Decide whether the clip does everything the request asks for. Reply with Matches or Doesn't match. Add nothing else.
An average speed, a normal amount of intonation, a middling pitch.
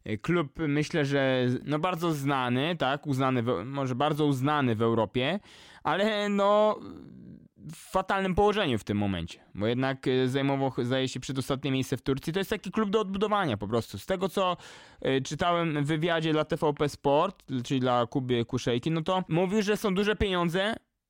Doesn't match